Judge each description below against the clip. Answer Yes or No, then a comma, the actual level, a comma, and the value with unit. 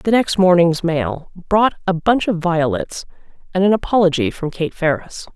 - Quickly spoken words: No, average, 170 wpm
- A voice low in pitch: No, medium, 175 Hz